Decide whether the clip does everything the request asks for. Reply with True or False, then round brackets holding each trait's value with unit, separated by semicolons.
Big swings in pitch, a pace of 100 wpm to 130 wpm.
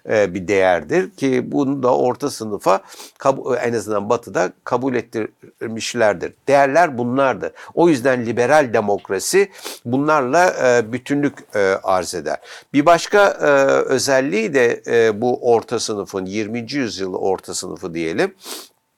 True (5.8 semitones; 110 wpm)